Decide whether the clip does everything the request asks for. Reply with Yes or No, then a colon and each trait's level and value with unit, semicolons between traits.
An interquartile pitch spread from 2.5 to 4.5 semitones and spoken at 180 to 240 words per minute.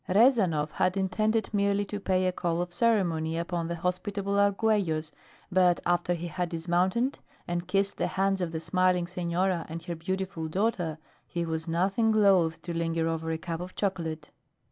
No: average, 2.9 semitones; average, 170 wpm